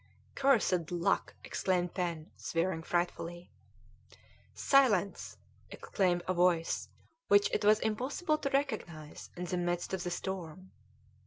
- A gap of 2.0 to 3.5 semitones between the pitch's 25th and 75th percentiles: Yes, average, 3.2 semitones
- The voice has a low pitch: No, medium, 180 Hz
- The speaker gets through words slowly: Yes, slow, 115 wpm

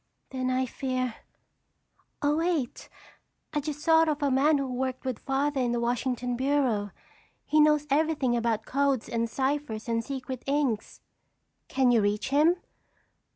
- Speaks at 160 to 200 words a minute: No, average, 145 wpm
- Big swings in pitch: No, average, 3.2 semitones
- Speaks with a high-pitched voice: Yes, very high, 265 Hz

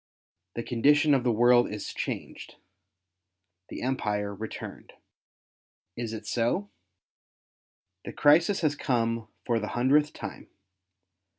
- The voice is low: Yes, low, 120 Hz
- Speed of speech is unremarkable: No, slow, 115 wpm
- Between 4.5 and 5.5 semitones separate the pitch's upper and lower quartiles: Yes, average, 4.9 semitones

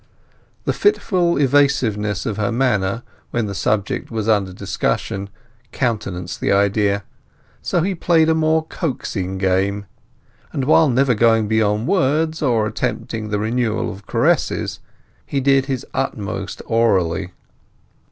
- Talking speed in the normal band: No, slow, 130 wpm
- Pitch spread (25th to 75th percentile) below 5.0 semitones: No, wide, 5.4 semitones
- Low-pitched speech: Yes, low, 110 Hz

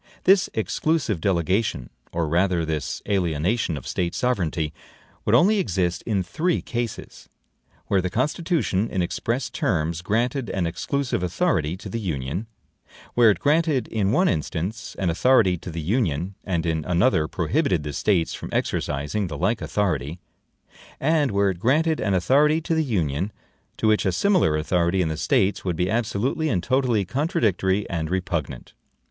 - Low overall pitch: Yes, very low, 95 Hz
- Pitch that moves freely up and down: Yes, wide, 6.3 semitones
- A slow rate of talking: No, average, 155 wpm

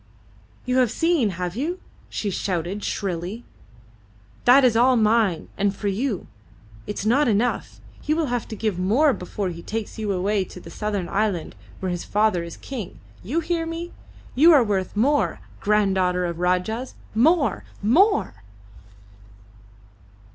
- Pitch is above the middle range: Yes, high, 215 Hz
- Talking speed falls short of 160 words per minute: Yes, average, 150 wpm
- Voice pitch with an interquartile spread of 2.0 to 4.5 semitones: No, wide, 5.5 semitones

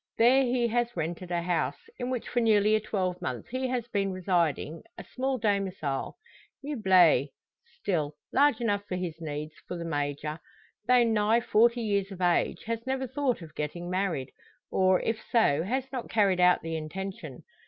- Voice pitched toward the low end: No, high, 195 Hz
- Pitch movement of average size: No, wide, 5.7 semitones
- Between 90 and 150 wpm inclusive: No, average, 170 wpm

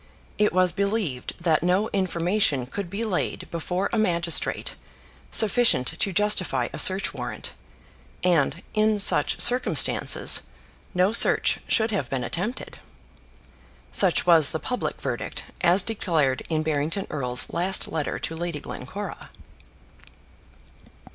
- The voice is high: No, medium, 180 Hz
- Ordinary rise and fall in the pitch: Yes, average, 4.4 semitones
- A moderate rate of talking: No, slow, 120 wpm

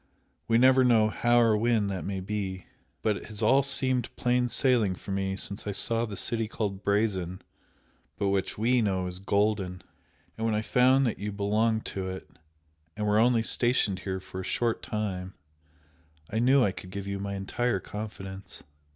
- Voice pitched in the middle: No, low, 105 Hz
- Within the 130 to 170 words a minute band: No, average, 185 wpm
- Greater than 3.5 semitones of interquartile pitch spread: No, average, 3.2 semitones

